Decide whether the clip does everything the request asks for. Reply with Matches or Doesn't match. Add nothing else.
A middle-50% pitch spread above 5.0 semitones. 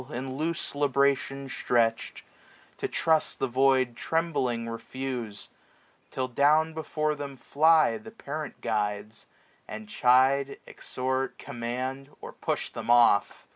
Doesn't match